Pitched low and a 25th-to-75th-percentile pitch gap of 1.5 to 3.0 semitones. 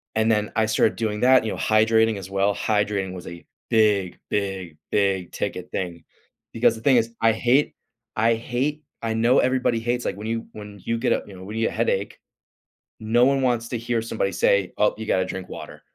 Yes: low, 110 Hz; narrow, 2.6 semitones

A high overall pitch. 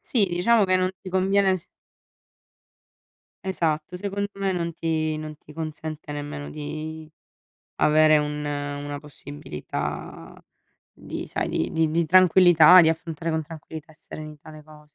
No: medium, 155 Hz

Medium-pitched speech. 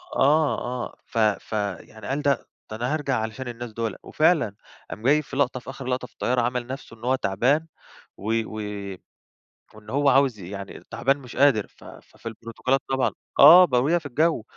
No: low, 125 Hz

